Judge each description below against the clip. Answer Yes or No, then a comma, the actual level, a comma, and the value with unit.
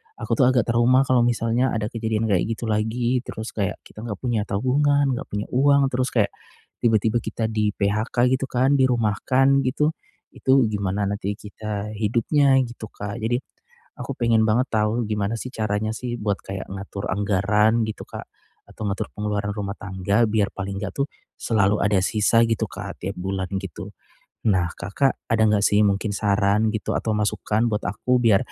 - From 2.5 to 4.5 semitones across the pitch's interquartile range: Yes, average, 2.8 semitones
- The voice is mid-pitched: No, low, 110 Hz